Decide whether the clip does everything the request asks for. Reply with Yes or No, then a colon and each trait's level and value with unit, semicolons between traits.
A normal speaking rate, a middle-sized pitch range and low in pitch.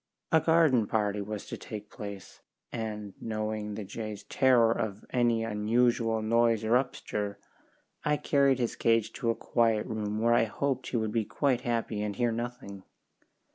No: average, 165 wpm; narrow, 2.3 semitones; low, 115 Hz